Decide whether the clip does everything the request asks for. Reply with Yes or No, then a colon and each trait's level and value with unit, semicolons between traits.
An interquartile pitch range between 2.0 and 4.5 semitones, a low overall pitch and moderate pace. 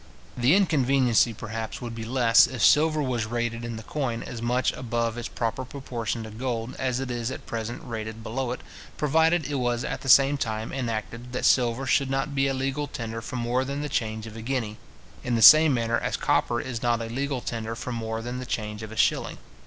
No: average, 2.7 semitones; low, 120 Hz; fast, 220 wpm